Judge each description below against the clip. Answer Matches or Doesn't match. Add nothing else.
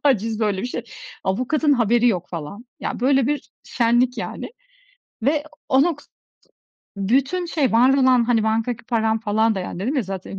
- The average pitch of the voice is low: Doesn't match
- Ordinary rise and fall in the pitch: Matches